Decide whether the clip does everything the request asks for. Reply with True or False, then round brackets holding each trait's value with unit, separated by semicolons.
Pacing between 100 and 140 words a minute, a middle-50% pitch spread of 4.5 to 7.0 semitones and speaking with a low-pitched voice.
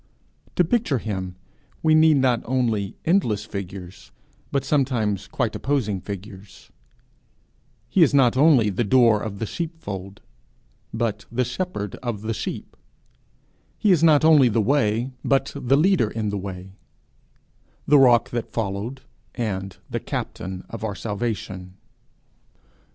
True (135 wpm; 5.3 semitones; 115 Hz)